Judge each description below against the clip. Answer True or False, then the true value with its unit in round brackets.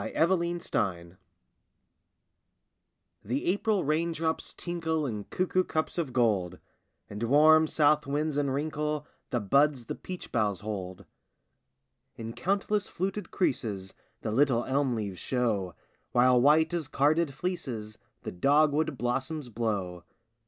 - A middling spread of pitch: False (6.3 semitones)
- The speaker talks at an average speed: False (120 wpm)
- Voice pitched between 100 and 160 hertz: True (140 Hz)